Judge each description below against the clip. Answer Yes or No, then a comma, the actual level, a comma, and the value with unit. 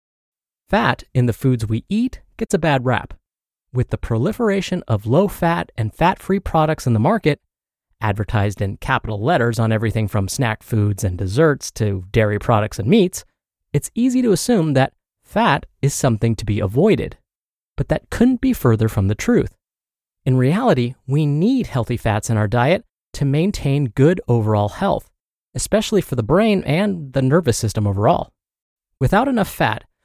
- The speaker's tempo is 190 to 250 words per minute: No, average, 170 wpm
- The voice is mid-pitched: No, low, 125 Hz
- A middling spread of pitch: No, wide, 7.5 semitones